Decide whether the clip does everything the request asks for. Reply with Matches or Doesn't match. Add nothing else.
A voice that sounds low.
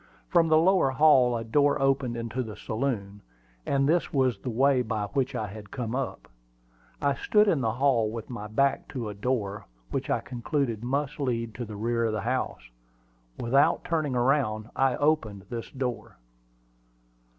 Matches